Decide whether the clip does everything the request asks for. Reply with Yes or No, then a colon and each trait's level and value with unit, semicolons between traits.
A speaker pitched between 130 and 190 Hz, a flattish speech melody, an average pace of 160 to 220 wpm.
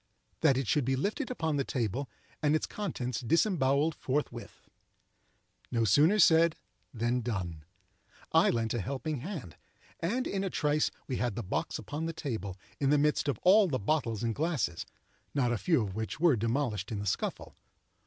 No: low, 135 Hz; wide, 5.6 semitones; average, 175 wpm